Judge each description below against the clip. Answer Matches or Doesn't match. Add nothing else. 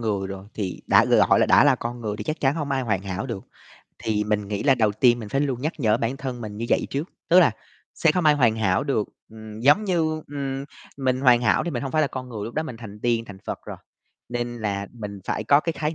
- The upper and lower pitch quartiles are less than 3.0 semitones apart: Doesn't match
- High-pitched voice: Doesn't match